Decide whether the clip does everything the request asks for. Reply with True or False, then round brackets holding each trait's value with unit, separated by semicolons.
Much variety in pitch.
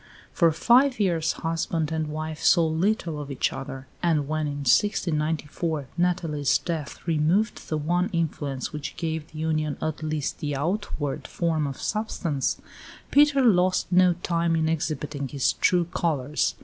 False (2.6 semitones)